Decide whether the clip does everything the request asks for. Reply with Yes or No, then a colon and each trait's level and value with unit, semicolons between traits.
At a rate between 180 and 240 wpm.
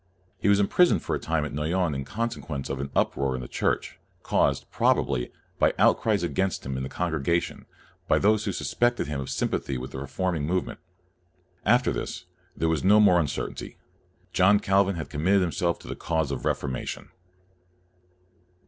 Yes: average, 185 wpm